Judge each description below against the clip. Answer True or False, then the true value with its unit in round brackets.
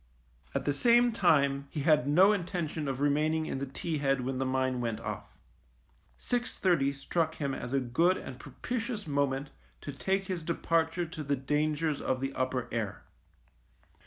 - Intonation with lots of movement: False (3.8 semitones)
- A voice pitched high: False (145 Hz)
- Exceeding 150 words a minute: True (170 wpm)